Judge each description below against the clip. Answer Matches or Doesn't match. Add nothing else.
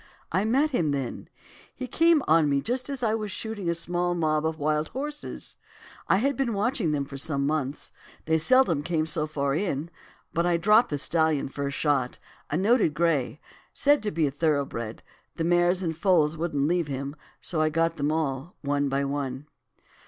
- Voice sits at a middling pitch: Matches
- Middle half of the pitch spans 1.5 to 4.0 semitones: Doesn't match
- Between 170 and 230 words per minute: Matches